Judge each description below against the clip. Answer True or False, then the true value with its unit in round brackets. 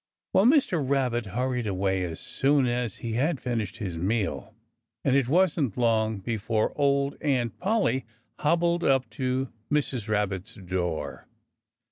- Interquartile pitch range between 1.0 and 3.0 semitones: False (5.1 semitones)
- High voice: False (125 Hz)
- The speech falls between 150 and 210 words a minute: False (135 wpm)